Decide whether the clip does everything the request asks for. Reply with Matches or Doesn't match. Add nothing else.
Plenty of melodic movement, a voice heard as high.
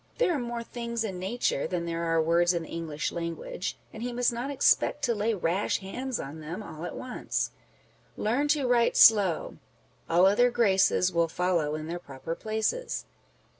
Matches